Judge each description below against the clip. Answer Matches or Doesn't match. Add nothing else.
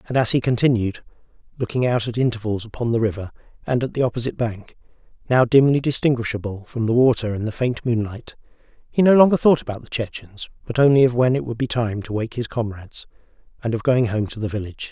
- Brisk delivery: Matches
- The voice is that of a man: Matches